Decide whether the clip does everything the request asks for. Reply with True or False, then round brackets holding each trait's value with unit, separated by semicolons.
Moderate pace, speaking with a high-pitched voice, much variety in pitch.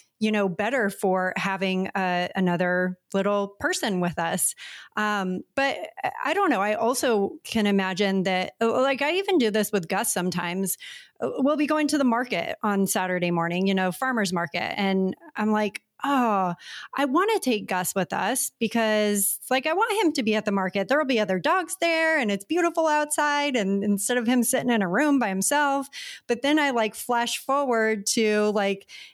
True (190 wpm; 215 Hz; 6.1 semitones)